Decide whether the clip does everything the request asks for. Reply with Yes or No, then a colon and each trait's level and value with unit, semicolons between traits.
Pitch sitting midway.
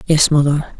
Yes: medium, 150 Hz